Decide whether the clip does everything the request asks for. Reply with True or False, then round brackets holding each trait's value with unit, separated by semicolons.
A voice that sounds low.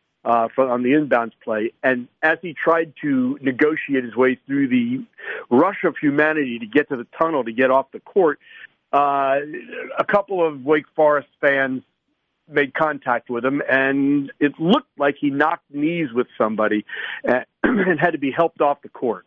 False (145 Hz)